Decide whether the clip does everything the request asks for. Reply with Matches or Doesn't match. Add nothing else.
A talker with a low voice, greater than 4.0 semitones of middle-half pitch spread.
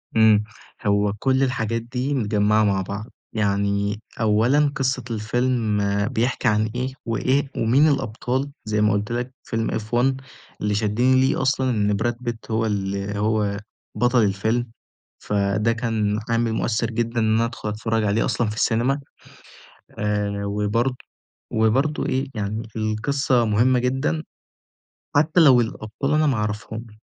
Doesn't match